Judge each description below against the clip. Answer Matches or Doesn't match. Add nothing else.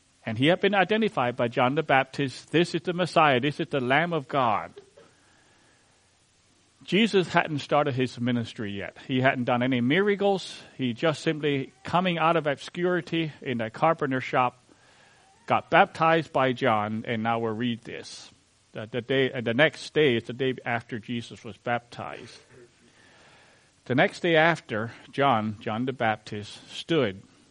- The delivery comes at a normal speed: Matches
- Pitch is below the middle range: Matches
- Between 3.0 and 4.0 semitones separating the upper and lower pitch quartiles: Doesn't match